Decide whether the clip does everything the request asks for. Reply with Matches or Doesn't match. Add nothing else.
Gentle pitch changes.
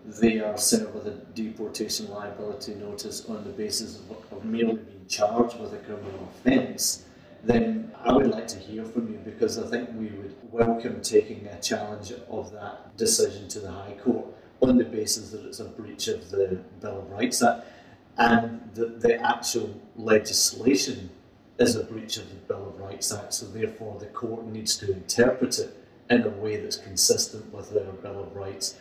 Doesn't match